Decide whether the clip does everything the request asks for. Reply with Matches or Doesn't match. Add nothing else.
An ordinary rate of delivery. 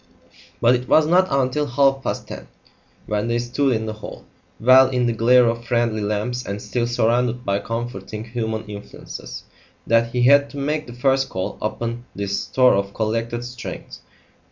Matches